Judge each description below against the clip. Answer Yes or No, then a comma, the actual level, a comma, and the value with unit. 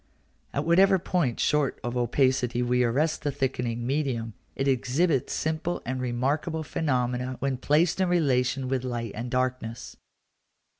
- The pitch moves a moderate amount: Yes, average, 3.6 semitones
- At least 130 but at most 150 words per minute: Yes, average, 140 wpm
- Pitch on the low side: Yes, low, 130 Hz